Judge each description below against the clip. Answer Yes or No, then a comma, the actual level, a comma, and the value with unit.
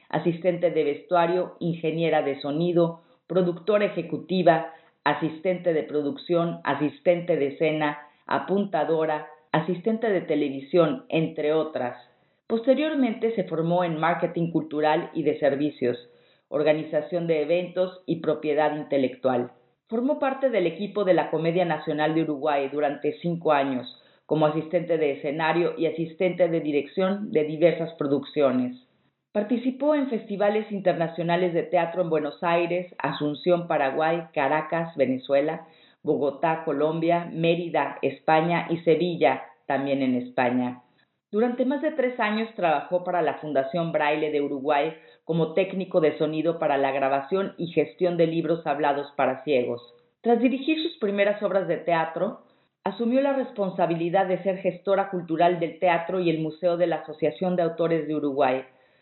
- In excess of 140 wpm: No, average, 135 wpm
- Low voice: No, medium, 165 Hz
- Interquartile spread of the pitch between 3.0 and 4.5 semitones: Yes, average, 3.3 semitones